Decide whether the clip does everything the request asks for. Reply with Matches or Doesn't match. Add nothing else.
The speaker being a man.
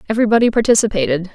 Doesn't match